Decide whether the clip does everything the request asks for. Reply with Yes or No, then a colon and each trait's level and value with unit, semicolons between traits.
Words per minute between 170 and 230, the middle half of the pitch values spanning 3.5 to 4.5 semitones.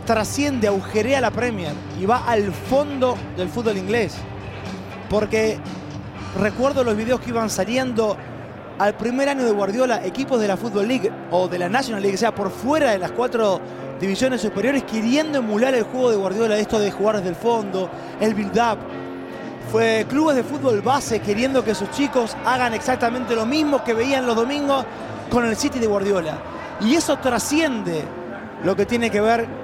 Yes: average, 175 wpm; average, 4.2 semitones